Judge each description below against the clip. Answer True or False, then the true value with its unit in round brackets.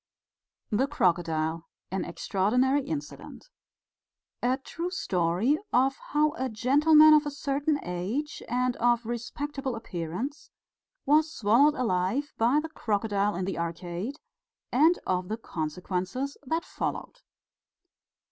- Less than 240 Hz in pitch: False (245 Hz)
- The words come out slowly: True (115 wpm)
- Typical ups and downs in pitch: False (7.6 semitones)